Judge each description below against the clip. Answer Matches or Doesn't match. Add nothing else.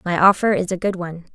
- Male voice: Doesn't match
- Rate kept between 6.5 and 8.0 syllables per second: Matches